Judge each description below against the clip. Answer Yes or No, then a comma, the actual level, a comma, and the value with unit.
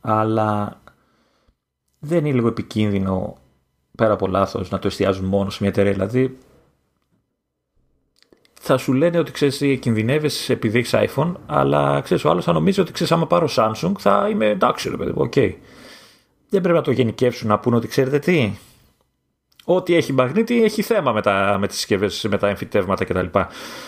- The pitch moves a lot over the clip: Yes, wide, 6.0 semitones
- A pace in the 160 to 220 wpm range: Yes, average, 165 wpm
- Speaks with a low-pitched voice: Yes, low, 110 Hz